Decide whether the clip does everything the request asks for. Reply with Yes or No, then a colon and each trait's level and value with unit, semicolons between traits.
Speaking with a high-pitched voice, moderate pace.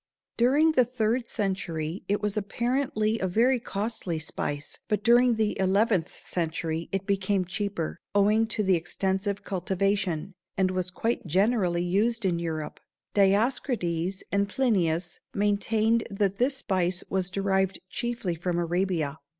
No: high, 195 Hz; slow, 130 wpm